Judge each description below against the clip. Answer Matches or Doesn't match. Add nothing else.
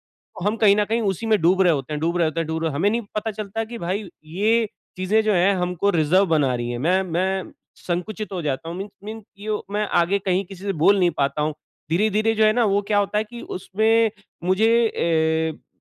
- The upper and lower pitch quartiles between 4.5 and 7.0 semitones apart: Doesn't match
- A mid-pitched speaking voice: Doesn't match